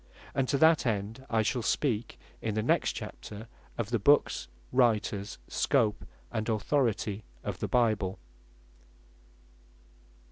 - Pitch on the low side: Yes, low, 110 Hz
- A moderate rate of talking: No, slow, 120 wpm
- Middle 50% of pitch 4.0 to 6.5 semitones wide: No, average, 2.9 semitones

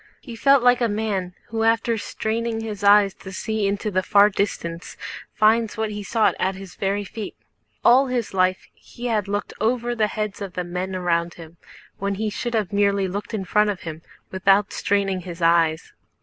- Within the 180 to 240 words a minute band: Yes, average, 190 wpm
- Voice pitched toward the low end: No, high, 205 Hz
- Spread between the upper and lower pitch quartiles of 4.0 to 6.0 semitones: No, average, 2.9 semitones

